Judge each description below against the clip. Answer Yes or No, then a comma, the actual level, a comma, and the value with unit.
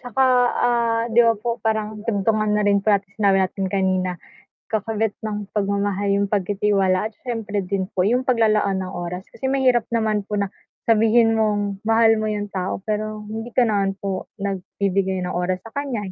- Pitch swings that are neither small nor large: No, narrow, 2.3 semitones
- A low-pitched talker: No, high, 210 Hz